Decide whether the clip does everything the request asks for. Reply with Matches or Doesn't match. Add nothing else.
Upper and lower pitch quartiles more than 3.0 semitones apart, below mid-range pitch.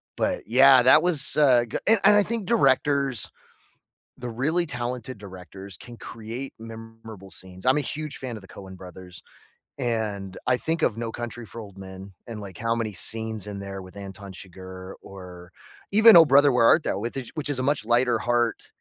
Matches